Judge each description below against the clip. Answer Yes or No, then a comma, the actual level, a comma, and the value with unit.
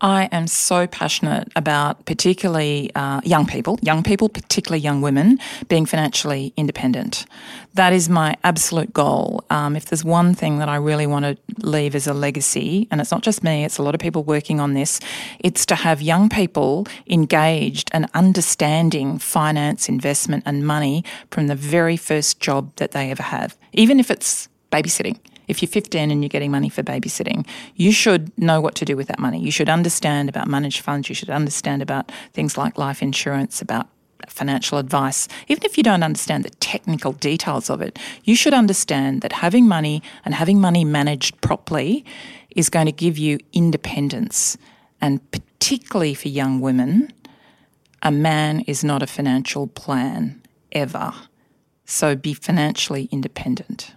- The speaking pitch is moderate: Yes, medium, 160 Hz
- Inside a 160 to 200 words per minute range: Yes, average, 170 wpm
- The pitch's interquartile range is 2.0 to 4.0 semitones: No, average, 4.7 semitones